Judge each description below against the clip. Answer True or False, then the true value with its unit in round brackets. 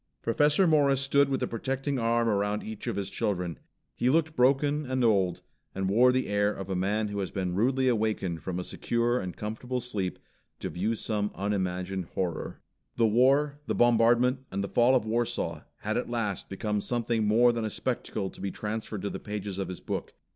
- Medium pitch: False (110 Hz)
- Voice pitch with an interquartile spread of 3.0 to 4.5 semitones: True (4.1 semitones)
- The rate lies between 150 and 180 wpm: False (195 wpm)